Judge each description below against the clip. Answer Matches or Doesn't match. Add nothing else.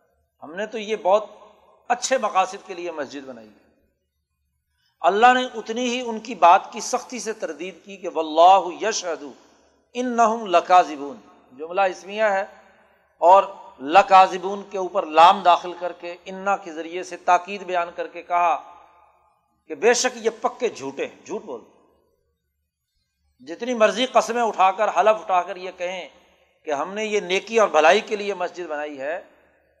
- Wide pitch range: Doesn't match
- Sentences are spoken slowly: Doesn't match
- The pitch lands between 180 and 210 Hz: Matches